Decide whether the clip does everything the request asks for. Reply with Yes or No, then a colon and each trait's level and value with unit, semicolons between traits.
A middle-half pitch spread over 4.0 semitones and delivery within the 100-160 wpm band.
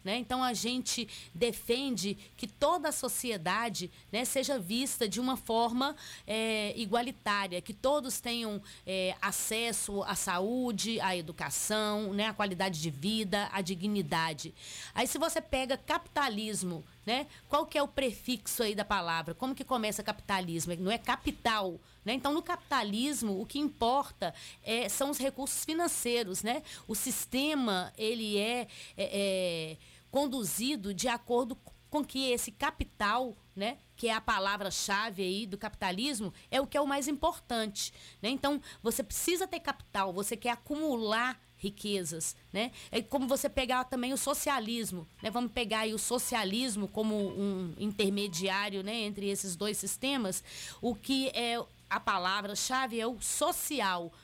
Yes: average, 4.5 semitones; average, 150 wpm